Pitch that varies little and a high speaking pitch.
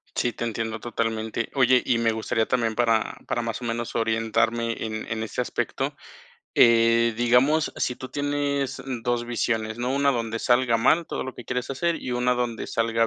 No: narrow, 1.8 semitones; low, 120 Hz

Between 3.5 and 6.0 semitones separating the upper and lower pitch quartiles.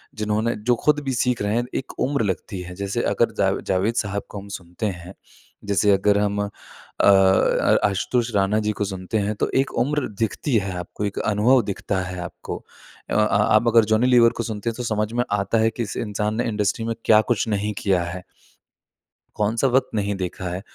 No: average, 2.8 semitones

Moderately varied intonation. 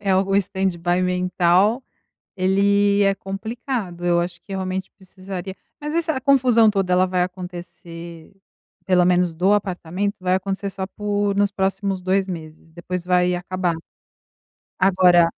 No: narrow, 1.9 semitones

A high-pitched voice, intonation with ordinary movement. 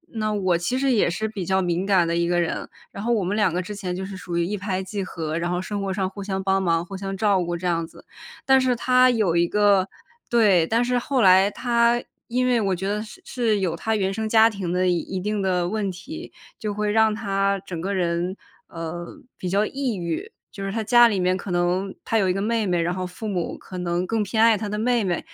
Yes: high, 195 Hz; average, 3.3 semitones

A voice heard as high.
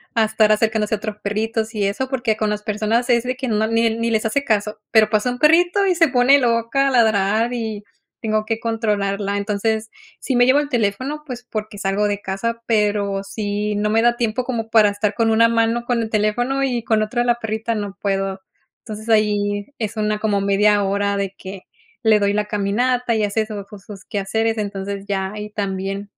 Yes: high, 215 Hz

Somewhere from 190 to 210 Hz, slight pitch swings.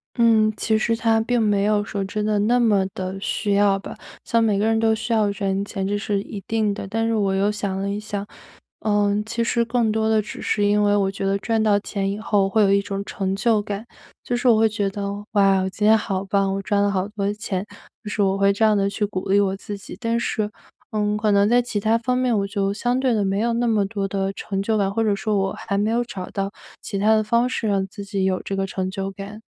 Yes: high, 205 Hz; narrow, 1.9 semitones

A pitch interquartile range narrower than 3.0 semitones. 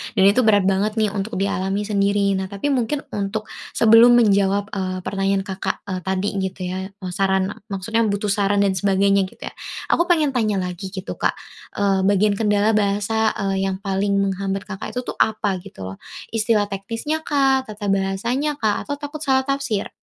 Yes: narrow, 2.4 semitones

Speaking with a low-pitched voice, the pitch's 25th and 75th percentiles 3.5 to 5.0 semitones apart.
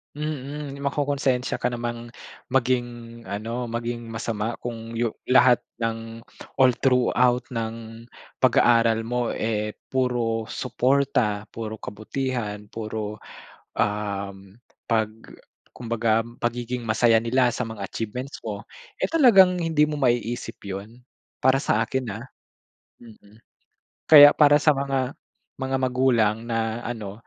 No: low, 120 Hz; average, 2.7 semitones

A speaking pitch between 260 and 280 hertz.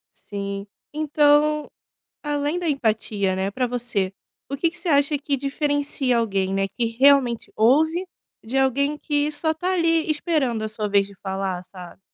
Yes: very high, 275 Hz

